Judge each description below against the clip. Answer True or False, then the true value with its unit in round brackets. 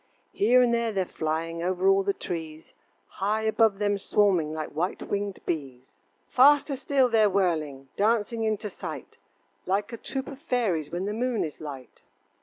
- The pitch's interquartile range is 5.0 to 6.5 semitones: True (5.5 semitones)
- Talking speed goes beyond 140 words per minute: True (165 wpm)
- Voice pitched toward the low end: False (200 Hz)